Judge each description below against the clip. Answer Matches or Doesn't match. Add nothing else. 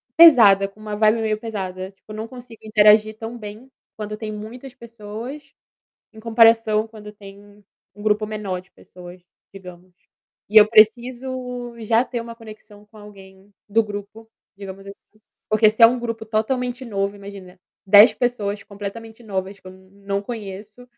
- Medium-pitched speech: Doesn't match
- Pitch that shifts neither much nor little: Doesn't match